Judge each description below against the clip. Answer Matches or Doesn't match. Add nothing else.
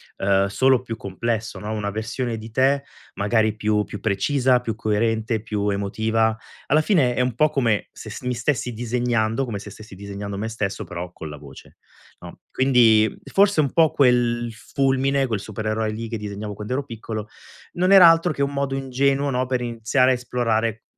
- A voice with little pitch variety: Doesn't match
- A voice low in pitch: Matches